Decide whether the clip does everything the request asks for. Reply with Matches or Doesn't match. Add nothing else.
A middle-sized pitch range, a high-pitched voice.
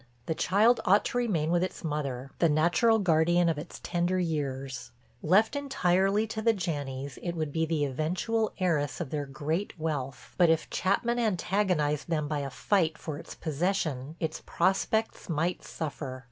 Doesn't match